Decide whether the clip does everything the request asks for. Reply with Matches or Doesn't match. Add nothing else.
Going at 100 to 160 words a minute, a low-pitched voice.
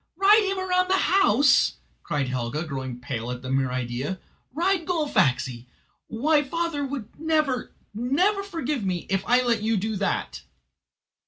Doesn't match